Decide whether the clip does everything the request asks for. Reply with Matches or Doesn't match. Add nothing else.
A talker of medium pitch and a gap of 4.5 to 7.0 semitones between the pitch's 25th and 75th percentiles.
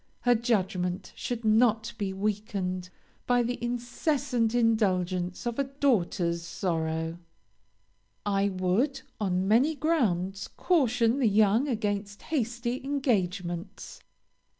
Doesn't match